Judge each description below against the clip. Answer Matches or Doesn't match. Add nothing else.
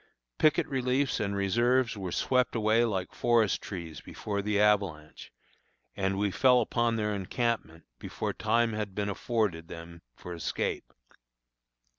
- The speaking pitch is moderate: Doesn't match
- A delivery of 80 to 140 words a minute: Matches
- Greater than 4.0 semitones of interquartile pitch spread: Doesn't match